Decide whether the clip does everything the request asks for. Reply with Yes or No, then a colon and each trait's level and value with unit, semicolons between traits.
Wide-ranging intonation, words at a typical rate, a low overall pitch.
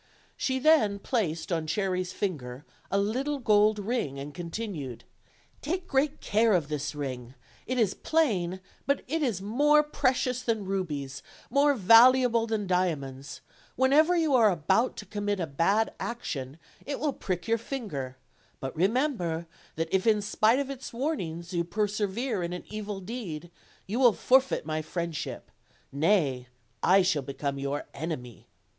No: wide, 7.4 semitones; average, 155 wpm; high, 200 Hz